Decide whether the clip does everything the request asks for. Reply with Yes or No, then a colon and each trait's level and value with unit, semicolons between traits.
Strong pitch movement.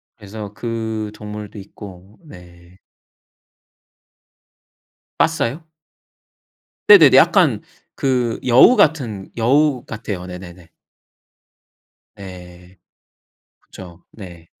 No: average, 4.4 semitones